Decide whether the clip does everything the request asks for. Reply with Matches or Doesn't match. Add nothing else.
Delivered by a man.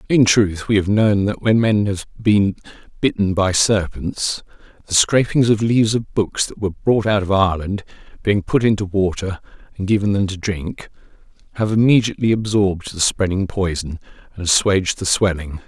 Matches